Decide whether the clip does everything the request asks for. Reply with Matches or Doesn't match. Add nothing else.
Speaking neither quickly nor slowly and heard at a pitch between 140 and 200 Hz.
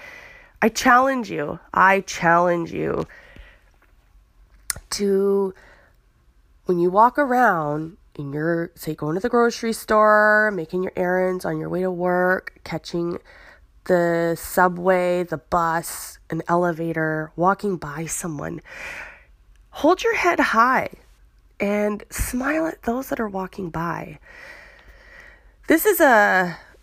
Doesn't match